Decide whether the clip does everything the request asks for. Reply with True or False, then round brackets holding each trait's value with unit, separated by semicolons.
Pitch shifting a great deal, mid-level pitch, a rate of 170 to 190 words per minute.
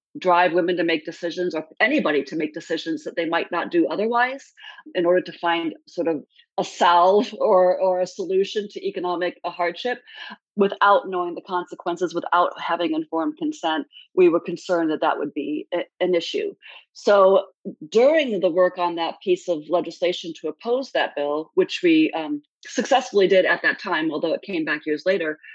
True (6.8 semitones; 180 Hz; 180 wpm)